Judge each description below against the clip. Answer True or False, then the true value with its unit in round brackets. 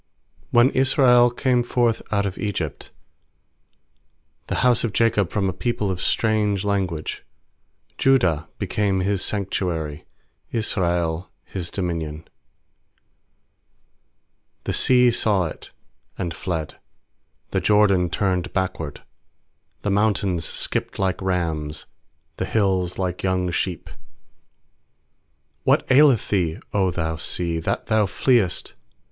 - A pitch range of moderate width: True (3.8 semitones)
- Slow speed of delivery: True (110 wpm)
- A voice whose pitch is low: True (95 Hz)